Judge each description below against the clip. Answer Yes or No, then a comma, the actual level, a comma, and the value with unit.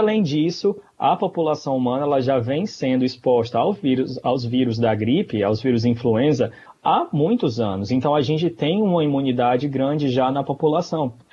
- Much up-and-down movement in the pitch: No, average, 3.9 semitones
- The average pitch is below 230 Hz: Yes, low, 135 Hz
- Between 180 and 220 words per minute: No, average, 170 wpm